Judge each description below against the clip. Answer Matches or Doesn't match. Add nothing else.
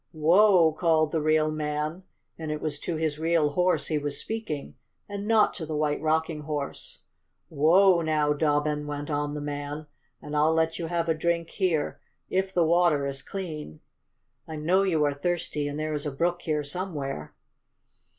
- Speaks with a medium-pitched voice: Matches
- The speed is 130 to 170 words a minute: Doesn't match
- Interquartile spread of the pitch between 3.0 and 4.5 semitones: Doesn't match